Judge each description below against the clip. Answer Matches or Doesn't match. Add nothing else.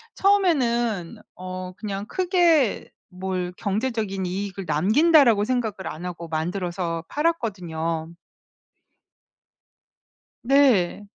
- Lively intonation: Matches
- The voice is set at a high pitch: Matches